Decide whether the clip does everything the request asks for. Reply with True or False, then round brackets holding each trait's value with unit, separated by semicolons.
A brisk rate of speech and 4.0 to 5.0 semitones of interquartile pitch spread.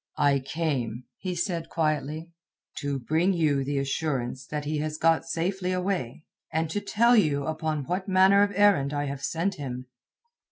False (165 wpm; 4.3 semitones)